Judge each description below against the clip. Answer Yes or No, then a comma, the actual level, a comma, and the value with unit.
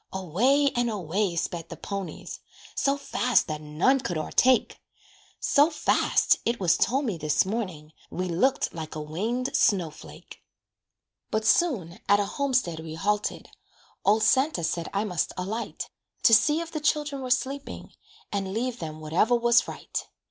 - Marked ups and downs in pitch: Yes, wide, 7.1 semitones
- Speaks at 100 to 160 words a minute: Yes, average, 155 wpm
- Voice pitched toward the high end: Yes, high, 210 Hz